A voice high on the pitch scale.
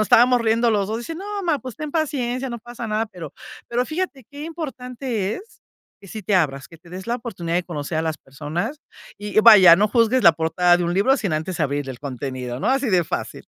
Yes: high, 215 Hz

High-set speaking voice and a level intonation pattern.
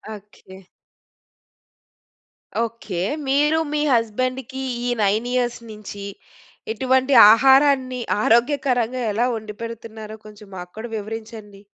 No: high, 230 Hz; average, 3.3 semitones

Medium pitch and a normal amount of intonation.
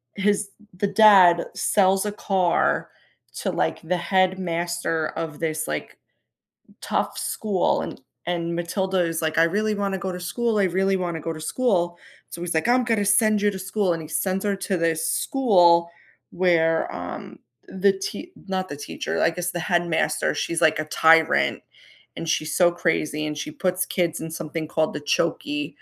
Yes: medium, 175 Hz; average, 3.1 semitones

